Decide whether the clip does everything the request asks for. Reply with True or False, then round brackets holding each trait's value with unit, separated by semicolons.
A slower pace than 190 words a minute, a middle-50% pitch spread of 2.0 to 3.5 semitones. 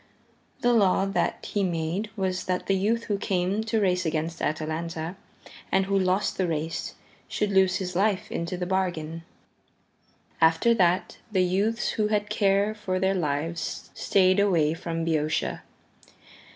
True (150 wpm; 3.2 semitones)